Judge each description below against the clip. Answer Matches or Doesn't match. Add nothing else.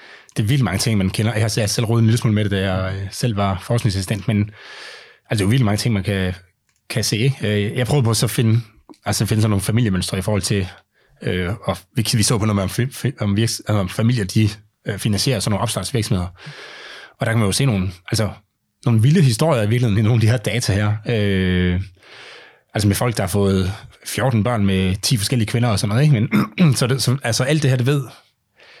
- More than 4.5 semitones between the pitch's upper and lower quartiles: Doesn't match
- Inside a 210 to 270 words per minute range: Matches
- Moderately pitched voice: Doesn't match